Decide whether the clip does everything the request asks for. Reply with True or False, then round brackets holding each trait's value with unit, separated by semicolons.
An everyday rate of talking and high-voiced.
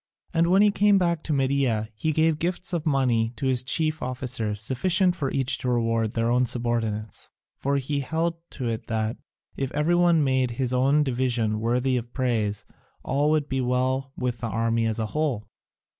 False (190 wpm; 130 Hz)